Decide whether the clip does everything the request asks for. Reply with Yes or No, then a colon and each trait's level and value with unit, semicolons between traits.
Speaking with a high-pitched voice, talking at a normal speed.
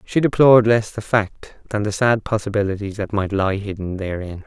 No: low, 105 Hz; average, 190 wpm